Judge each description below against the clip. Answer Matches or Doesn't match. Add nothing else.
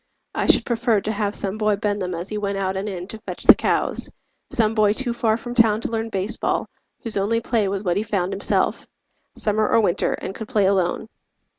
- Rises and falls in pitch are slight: Matches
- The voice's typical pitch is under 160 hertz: Doesn't match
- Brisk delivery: Matches